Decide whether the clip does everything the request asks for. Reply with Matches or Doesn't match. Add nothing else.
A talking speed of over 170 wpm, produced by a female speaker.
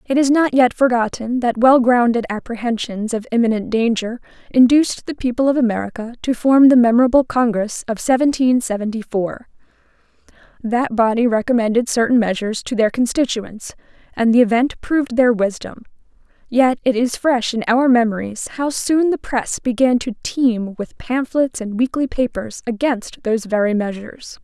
Doesn't match